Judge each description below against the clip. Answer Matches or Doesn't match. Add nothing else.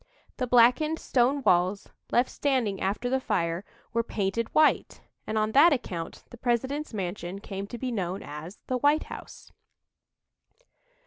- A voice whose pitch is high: Matches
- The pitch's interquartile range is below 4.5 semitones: Doesn't match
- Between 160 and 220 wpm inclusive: Doesn't match